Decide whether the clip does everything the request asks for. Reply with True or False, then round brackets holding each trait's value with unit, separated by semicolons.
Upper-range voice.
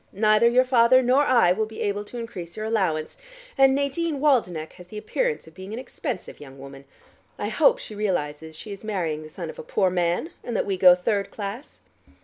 True (210 Hz)